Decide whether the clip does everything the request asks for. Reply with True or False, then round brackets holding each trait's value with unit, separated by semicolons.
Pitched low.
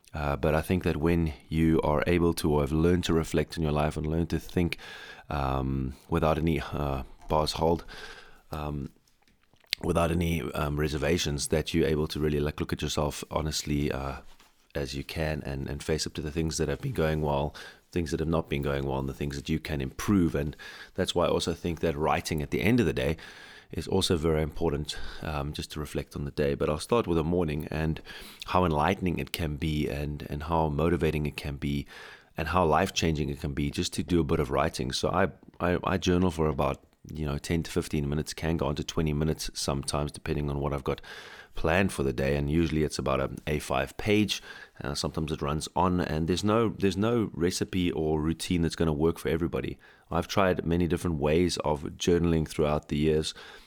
True (80 Hz)